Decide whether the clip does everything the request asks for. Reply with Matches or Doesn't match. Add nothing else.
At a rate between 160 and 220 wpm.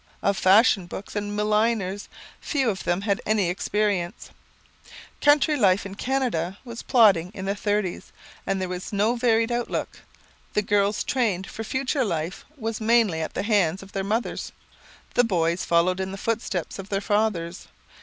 Matches